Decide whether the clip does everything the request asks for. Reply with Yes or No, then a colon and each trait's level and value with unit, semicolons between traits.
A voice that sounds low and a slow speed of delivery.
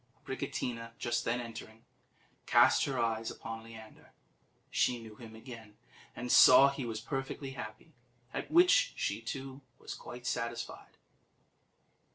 Yes: low, 120 Hz; slow, 130 wpm